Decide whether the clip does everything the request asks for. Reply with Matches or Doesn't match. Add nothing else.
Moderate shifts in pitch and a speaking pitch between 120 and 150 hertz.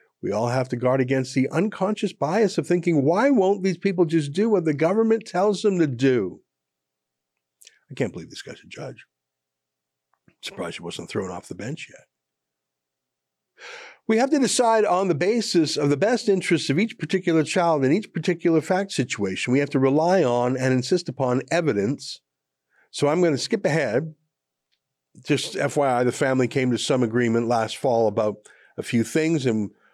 Doesn't match